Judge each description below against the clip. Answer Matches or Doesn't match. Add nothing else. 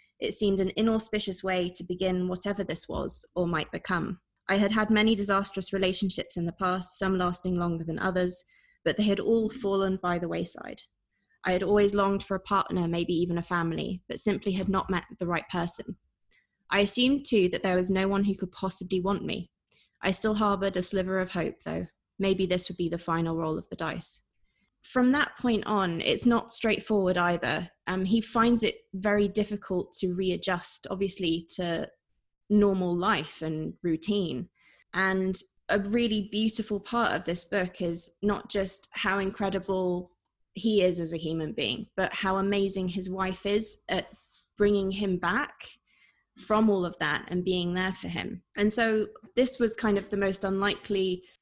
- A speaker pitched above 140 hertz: Matches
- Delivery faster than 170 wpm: Matches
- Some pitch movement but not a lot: Doesn't match